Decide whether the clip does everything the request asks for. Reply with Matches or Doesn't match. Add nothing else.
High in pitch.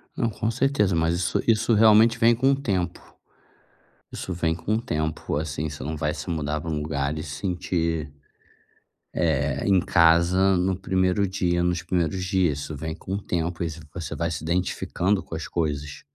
Doesn't match